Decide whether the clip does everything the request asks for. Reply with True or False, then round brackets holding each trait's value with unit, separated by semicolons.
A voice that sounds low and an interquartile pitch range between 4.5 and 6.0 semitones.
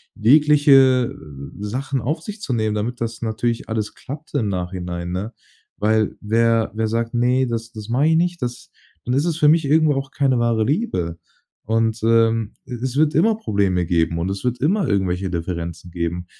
True (115 Hz; 5.6 semitones)